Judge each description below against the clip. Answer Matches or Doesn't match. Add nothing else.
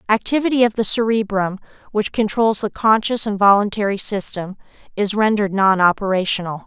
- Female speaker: Matches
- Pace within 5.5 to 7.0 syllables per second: Matches